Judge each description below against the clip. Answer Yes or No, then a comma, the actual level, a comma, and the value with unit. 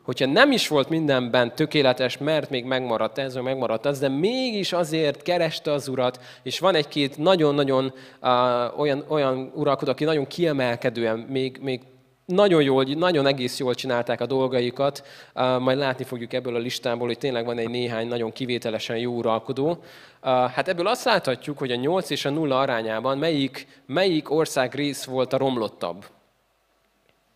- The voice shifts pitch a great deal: No, average, 2.8 semitones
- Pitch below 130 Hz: No, low, 135 Hz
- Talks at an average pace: No, fast, 165 wpm